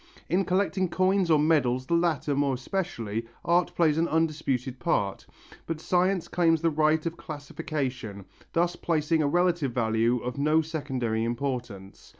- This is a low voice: No, medium, 155 Hz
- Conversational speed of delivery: Yes, average, 150 wpm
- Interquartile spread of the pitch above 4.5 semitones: Yes, average, 5.1 semitones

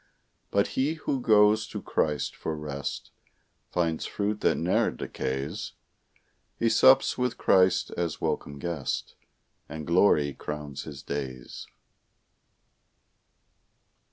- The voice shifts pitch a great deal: Yes, wide, 6.5 semitones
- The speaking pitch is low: Yes, very low, 85 Hz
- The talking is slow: Yes, slow, 105 wpm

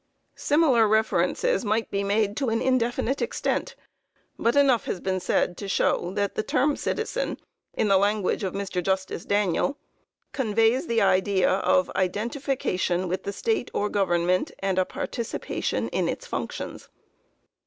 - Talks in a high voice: Yes, high, 205 Hz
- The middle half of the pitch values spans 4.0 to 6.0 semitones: Yes, average, 4.9 semitones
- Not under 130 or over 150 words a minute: Yes, average, 145 wpm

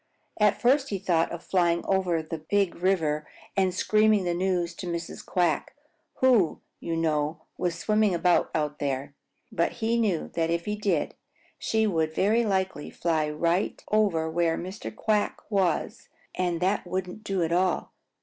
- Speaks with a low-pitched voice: No, medium, 180 Hz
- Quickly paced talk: No, average, 165 wpm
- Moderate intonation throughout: Yes, average, 3.6 semitones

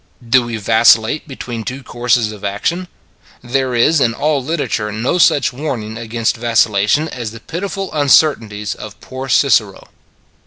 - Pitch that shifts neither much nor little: Yes, average, 4.0 semitones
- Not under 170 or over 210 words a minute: No, average, 145 wpm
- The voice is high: No, low, 120 Hz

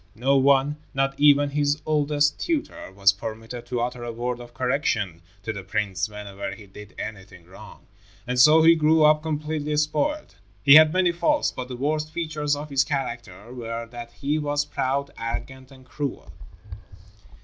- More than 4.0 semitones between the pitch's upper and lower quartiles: Yes, average, 4.4 semitones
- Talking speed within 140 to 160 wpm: No, average, 170 wpm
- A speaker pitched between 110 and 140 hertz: Yes, low, 135 Hz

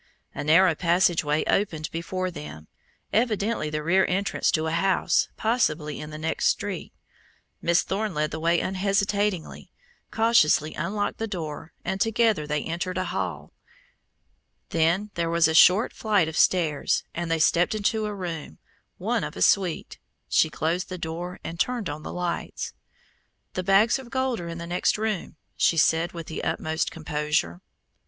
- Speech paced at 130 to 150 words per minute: No, average, 165 wpm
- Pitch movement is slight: No, average, 3.8 semitones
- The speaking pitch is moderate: Yes, medium, 175 Hz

